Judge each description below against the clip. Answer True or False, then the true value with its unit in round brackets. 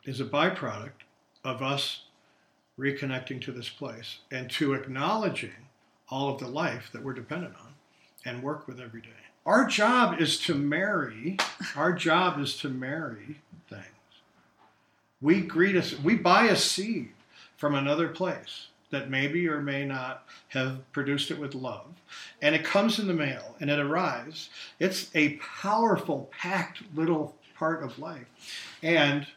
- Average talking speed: True (150 wpm)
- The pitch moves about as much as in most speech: True (3.7 semitones)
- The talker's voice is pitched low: False (145 Hz)